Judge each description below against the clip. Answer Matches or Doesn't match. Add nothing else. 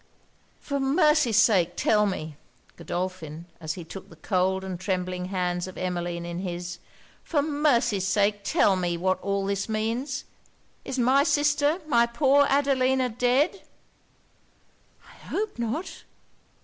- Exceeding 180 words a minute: Doesn't match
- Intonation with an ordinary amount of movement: Doesn't match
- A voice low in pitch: Doesn't match